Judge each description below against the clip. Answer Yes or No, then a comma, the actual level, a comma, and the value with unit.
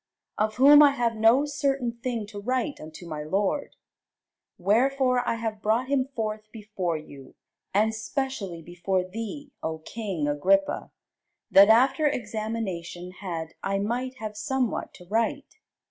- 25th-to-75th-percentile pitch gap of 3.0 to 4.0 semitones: No, average, 5.3 semitones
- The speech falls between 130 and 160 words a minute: Yes, average, 140 wpm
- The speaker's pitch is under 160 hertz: No, high, 220 Hz